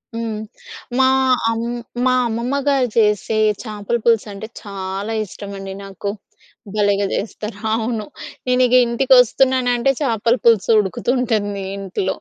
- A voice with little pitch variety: No, average, 3.3 semitones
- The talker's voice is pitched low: No, high, 225 Hz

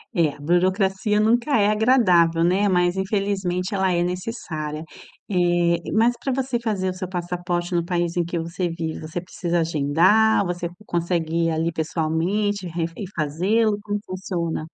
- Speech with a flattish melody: No, average, 3.3 semitones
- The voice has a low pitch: No, medium, 180 Hz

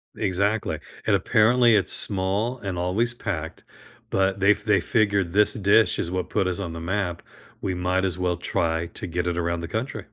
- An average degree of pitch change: Yes, average, 3.1 semitones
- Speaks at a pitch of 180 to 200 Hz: No, very low, 95 Hz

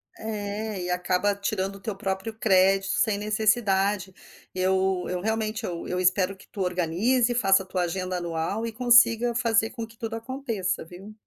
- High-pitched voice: Yes, high, 200 Hz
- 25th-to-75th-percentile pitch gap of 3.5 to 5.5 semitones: No, average, 3.1 semitones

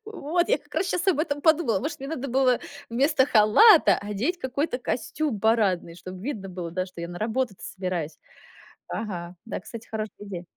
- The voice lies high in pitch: Yes, high, 230 Hz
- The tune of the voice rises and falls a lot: Yes, wide, 7.5 semitones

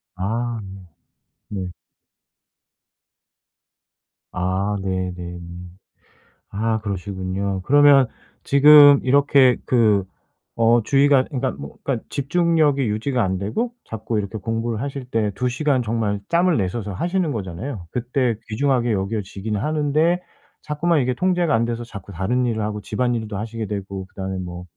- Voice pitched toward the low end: Yes, low, 115 Hz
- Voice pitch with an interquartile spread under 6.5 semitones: Yes, wide, 5.7 semitones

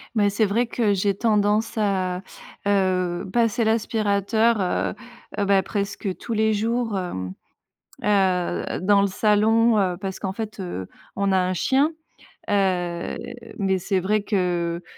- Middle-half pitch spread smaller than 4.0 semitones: Yes, average, 2.7 semitones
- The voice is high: Yes, high, 200 Hz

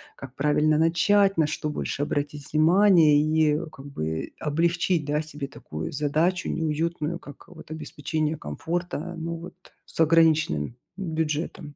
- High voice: No, medium, 155 Hz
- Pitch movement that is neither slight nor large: No, narrow, 2.2 semitones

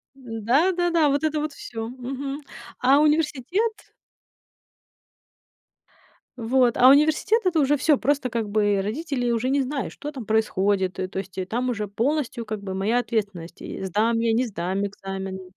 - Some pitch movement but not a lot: No, wide, 5.8 semitones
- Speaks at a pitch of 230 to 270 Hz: Yes, high, 245 Hz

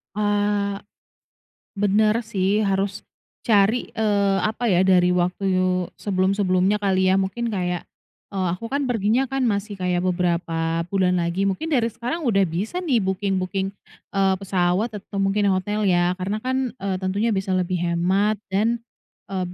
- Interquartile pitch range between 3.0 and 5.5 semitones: No, narrow, 2.5 semitones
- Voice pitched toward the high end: Yes, high, 195 Hz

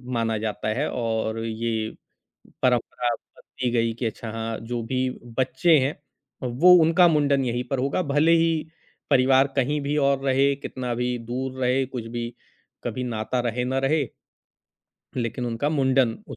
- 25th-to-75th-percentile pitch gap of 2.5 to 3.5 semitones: Yes, average, 2.8 semitones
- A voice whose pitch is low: Yes, low, 125 Hz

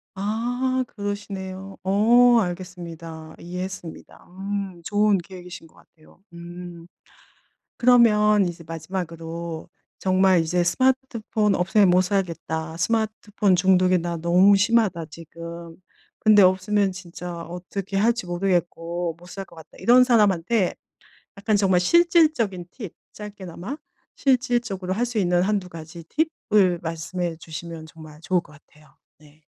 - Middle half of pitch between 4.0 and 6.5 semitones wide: No, average, 3.6 semitones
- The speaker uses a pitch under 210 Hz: Yes, medium, 185 Hz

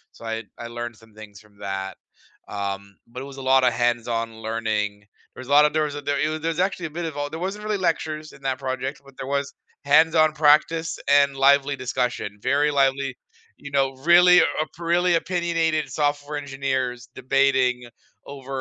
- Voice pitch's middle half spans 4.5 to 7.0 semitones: No, average, 4.1 semitones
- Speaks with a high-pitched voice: No, medium, 140 Hz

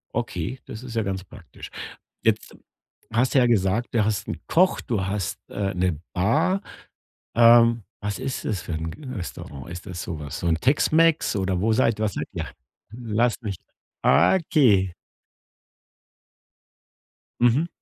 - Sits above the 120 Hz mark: No, low, 110 Hz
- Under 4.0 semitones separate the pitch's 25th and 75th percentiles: No, average, 4.6 semitones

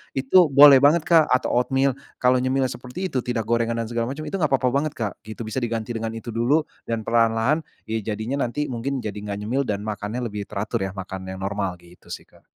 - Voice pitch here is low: Yes, low, 120 Hz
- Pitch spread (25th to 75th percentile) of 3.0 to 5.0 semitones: Yes, average, 3.8 semitones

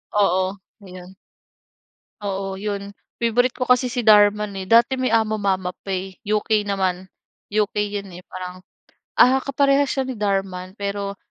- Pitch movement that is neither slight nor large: Yes, average, 3.0 semitones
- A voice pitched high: Yes, high, 200 Hz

